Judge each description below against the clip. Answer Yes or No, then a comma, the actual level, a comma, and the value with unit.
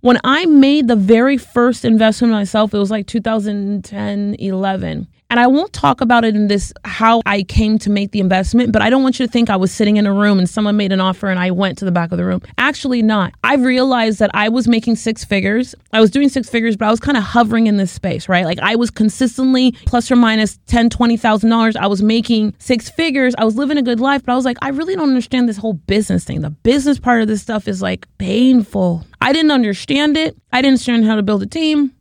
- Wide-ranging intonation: No, average, 3.6 semitones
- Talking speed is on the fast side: Yes, fast, 255 wpm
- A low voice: No, high, 225 Hz